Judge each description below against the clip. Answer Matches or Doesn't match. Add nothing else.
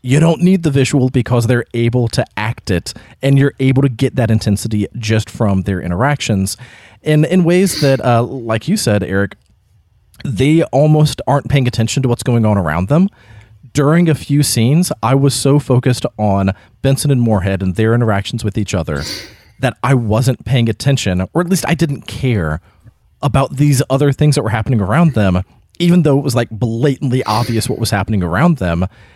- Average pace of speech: Matches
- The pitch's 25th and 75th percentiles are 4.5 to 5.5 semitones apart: Matches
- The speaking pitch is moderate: Doesn't match